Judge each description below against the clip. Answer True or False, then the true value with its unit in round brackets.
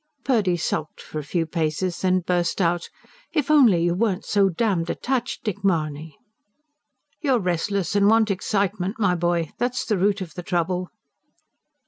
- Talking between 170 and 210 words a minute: False (155 wpm)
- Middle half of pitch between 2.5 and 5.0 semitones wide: True (3.4 semitones)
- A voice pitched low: False (185 Hz)